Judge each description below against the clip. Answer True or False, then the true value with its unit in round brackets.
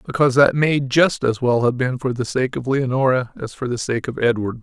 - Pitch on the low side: True (130 Hz)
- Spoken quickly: True (245 wpm)